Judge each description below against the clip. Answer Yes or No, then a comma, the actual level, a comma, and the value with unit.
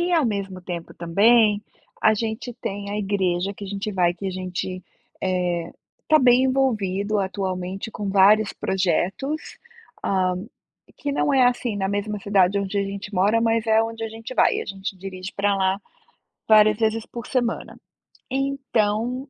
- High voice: Yes, high, 205 Hz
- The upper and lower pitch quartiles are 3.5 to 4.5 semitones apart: No, average, 3.0 semitones